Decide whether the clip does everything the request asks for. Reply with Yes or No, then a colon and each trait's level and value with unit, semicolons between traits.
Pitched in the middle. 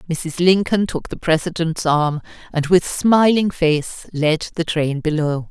Yes: medium, 165 Hz